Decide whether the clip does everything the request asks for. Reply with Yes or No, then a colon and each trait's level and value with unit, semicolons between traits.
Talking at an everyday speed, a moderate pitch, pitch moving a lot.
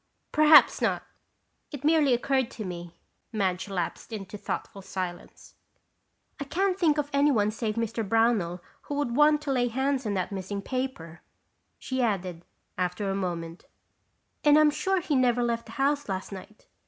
No: average, 160 wpm; high, 230 Hz; wide, 6.7 semitones